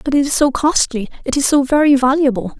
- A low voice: No, very high, 270 Hz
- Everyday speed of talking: No, fast, 210 wpm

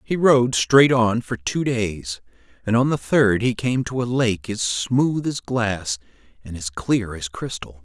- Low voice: Yes, low, 110 Hz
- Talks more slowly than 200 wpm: Yes, average, 190 wpm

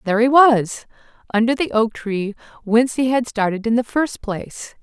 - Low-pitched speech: No, high, 230 Hz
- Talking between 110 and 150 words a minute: No, average, 185 wpm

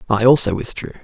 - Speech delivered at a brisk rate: No, average, 175 wpm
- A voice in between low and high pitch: No, low, 115 Hz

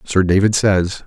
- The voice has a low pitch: Yes, very low, 95 Hz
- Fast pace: No, average, 170 wpm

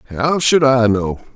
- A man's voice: Yes, male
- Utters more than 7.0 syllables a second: No, 3.9 syllables/s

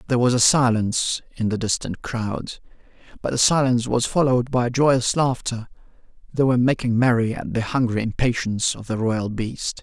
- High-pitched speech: No, low, 120 Hz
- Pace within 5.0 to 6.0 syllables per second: Yes, 5.3 syllables/s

